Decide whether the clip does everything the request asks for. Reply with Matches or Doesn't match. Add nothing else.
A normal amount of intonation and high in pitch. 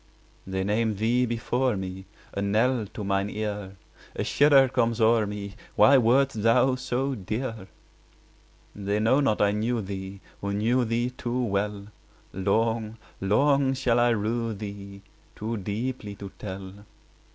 Doesn't match